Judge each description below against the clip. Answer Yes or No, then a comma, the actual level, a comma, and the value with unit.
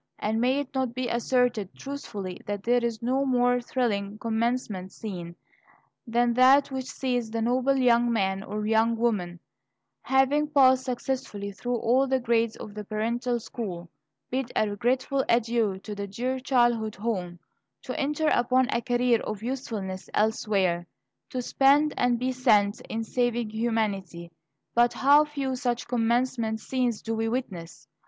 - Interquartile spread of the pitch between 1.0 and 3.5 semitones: Yes, average, 3.2 semitones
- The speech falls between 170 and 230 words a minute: No, average, 150 wpm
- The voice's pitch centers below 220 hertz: No, high, 235 Hz